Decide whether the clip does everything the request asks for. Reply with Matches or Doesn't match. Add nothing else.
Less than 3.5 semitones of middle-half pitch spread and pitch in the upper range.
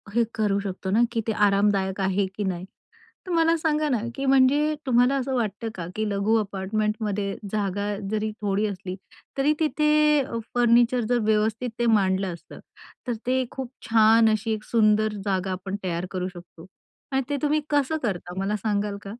Doesn't match